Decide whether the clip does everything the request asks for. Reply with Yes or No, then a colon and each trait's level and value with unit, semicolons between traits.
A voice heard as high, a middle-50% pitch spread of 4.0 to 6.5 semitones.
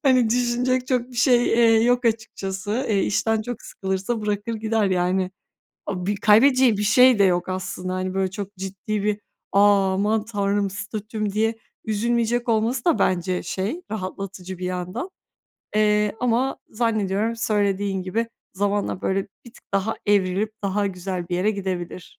No: high, 205 Hz; average, 3.1 semitones